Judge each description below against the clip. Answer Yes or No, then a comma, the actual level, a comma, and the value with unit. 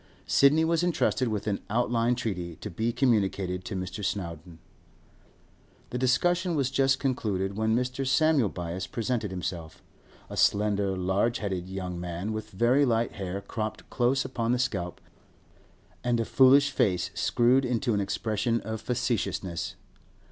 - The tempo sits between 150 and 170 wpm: No, average, 140 wpm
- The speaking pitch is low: Yes, low, 110 Hz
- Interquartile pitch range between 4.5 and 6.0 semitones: Yes, average, 4.8 semitones